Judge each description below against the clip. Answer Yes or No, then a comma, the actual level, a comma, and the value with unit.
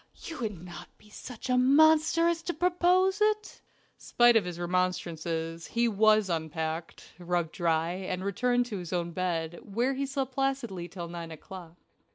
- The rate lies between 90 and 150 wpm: No, average, 160 wpm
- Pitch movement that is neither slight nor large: No, wide, 7.7 semitones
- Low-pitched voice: No, high, 195 Hz